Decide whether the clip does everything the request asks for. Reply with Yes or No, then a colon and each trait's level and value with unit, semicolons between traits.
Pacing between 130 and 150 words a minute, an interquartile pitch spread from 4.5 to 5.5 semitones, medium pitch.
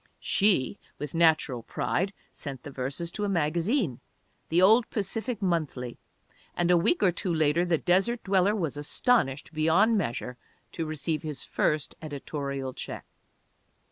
Yes: average, 140 wpm; average, 5.0 semitones; medium, 165 Hz